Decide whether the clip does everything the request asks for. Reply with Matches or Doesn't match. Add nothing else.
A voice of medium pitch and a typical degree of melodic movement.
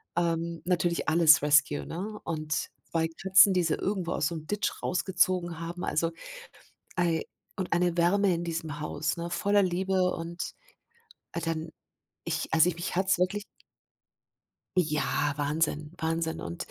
Doesn't match